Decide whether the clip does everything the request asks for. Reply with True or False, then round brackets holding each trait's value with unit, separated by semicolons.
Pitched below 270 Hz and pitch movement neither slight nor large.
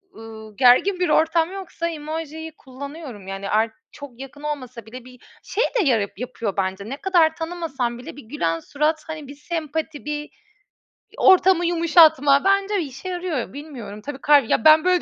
False (295 Hz; 4.8 semitones)